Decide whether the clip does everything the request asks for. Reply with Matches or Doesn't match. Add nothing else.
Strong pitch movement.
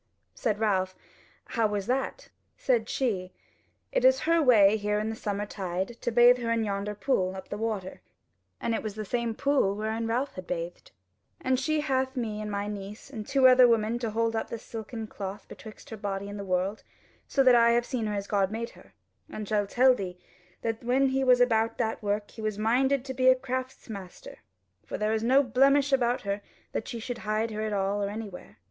Doesn't match